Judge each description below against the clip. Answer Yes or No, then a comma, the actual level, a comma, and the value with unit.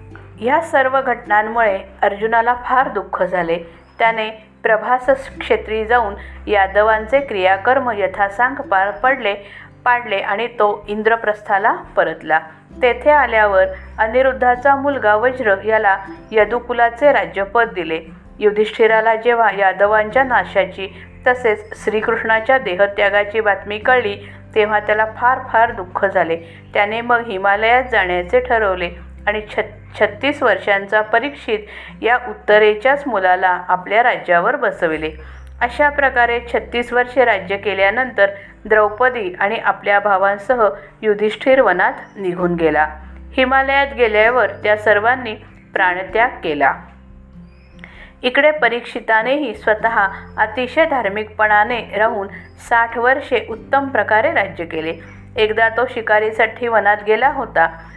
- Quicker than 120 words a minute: No, average, 100 wpm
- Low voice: No, high, 215 Hz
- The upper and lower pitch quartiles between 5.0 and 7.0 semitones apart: No, average, 3.8 semitones